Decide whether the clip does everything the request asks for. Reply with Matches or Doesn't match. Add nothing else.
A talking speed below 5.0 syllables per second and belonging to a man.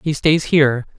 Doesn't match